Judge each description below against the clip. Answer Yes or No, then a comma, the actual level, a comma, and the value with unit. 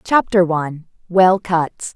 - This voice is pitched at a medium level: Yes, medium, 180 Hz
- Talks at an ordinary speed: No, slow, 90 wpm